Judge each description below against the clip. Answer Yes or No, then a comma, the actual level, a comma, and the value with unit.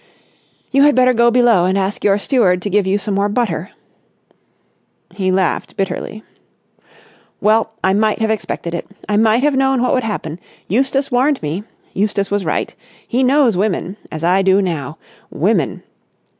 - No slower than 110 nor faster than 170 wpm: Yes, average, 160 wpm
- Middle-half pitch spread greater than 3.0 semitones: Yes, average, 4.5 semitones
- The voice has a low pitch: No, high, 205 Hz